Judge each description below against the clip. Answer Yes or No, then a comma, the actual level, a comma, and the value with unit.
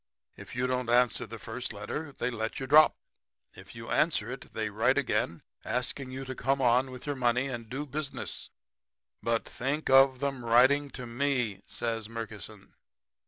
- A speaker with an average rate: Yes, average, 170 wpm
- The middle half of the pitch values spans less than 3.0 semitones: Yes, narrow, 2.6 semitones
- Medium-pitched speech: No, low, 125 Hz